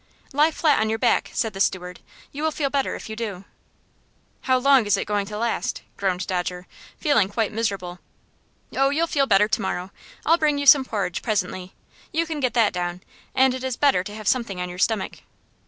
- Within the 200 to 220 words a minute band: Yes, fast, 205 wpm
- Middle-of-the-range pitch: No, high, 220 Hz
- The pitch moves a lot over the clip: Yes, wide, 6.2 semitones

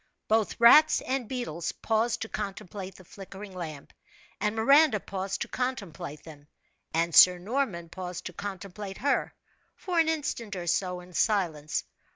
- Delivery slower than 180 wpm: Yes, average, 150 wpm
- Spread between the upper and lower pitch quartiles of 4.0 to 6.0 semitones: Yes, average, 4.7 semitones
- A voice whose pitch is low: No, high, 195 Hz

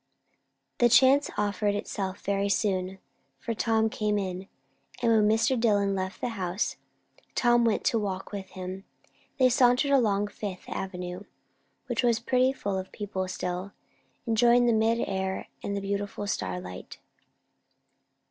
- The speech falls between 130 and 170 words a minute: Yes, slow, 135 wpm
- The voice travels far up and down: No, average, 3.4 semitones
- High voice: Yes, high, 205 Hz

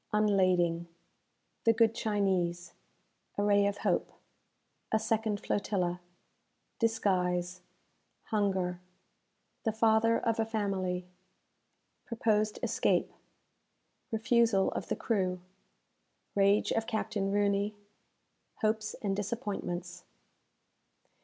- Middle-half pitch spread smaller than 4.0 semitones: Yes, average, 2.9 semitones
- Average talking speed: No, slow, 90 wpm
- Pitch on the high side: Yes, high, 205 Hz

